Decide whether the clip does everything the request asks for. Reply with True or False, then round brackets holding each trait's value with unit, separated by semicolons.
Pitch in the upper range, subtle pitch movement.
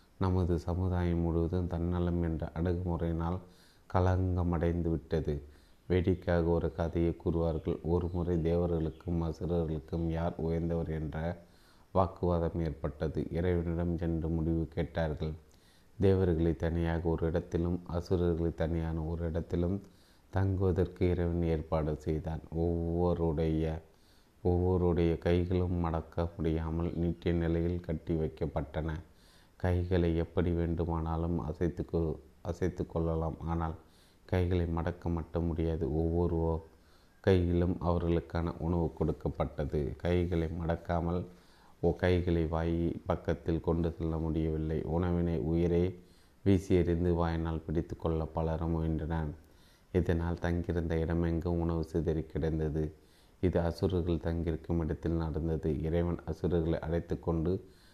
False (85 Hz; 1.3 semitones)